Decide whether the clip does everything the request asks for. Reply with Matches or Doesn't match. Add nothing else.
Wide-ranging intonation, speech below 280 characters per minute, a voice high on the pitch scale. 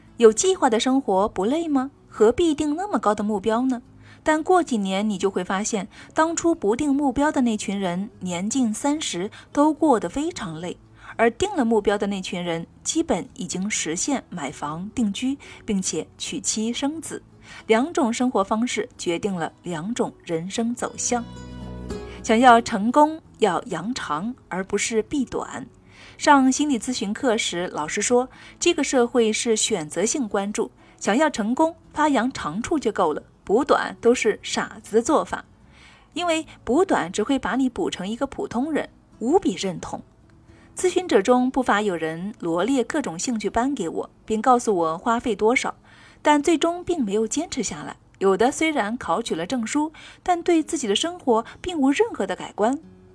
Matches